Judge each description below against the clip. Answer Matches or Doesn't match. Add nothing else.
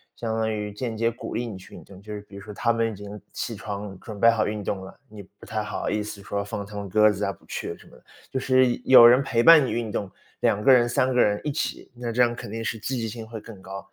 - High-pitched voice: Doesn't match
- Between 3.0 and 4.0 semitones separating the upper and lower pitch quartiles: Doesn't match